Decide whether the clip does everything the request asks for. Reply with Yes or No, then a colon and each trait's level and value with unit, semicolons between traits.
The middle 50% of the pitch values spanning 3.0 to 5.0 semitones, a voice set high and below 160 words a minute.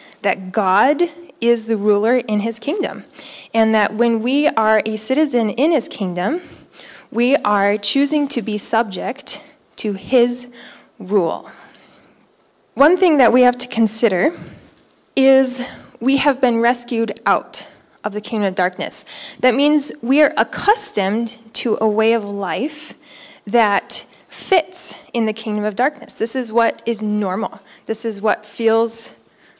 Yes: average, 3.8 semitones; high, 230 Hz; average, 145 wpm